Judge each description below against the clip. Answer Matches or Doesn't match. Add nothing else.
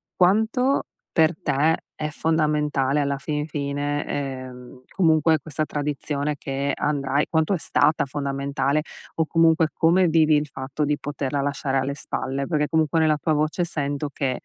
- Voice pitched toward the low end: Doesn't match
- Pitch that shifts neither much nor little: Doesn't match